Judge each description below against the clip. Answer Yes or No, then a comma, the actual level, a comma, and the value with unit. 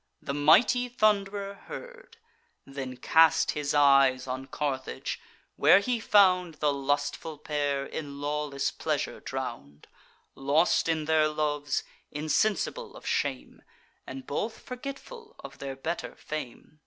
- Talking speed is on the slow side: Yes, slow, 120 wpm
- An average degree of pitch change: No, wide, 6.3 semitones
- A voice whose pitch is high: No, medium, 150 Hz